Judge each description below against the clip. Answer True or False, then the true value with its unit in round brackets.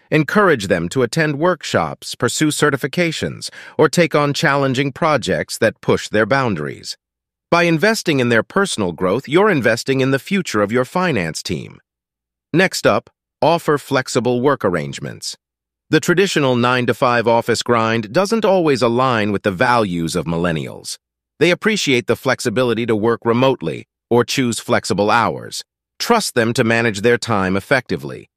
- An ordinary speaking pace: True (150 wpm)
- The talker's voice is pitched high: False (125 Hz)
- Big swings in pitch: True (5.7 semitones)